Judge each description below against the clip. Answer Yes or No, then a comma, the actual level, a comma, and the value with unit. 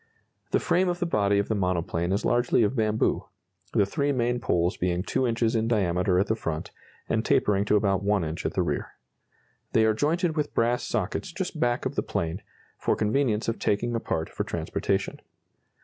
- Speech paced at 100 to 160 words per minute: No, average, 195 wpm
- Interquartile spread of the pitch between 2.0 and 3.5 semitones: No, average, 3.9 semitones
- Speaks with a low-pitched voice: Yes, low, 110 Hz